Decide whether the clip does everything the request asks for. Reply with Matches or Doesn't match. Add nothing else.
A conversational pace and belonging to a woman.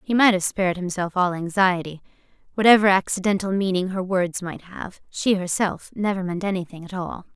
Matches